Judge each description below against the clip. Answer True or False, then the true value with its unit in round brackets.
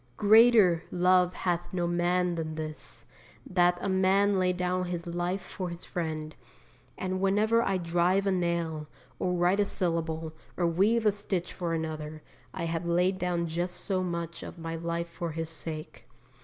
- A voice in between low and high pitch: True (175 Hz)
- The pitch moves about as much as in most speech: False (1.9 semitones)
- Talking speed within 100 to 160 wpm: False (170 wpm)